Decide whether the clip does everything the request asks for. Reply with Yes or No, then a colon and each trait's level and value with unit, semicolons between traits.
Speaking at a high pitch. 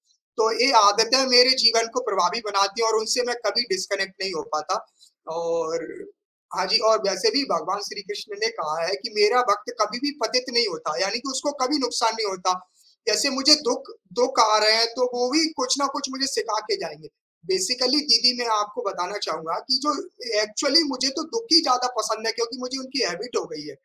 Yes: high, 235 Hz